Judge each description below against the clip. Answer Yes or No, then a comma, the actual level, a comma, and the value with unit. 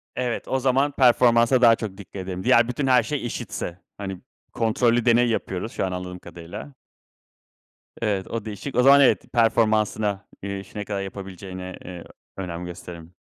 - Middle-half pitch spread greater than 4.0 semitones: Yes, average, 4.4 semitones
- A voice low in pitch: Yes, low, 105 Hz